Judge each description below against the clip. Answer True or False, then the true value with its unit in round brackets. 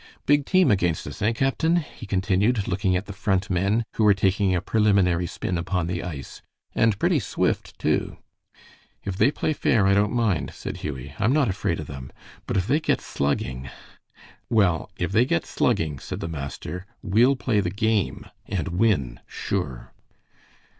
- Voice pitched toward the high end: False (95 Hz)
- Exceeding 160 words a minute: True (175 wpm)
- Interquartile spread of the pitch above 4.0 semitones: True (4.5 semitones)